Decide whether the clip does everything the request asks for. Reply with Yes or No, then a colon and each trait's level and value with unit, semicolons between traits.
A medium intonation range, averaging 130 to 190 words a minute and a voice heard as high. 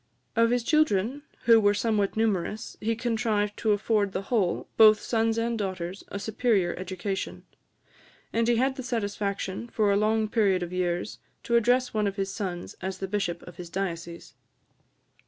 Yes: average, 3.1 semitones; average, 170 wpm; high, 210 Hz